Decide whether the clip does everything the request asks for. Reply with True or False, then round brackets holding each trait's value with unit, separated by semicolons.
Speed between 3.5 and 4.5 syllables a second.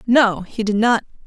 True (4.4 syllables/s)